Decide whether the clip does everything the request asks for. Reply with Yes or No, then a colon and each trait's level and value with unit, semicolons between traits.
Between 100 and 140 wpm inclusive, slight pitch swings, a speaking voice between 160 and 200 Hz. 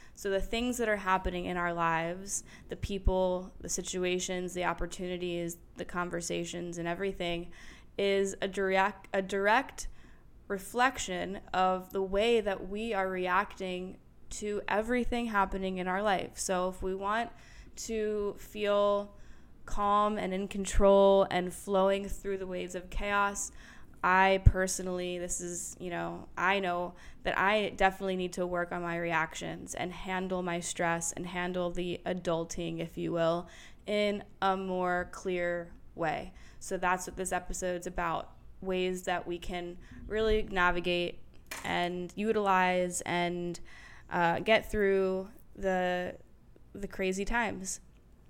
Yes: slow, 135 wpm; narrow, 2.0 semitones; medium, 185 Hz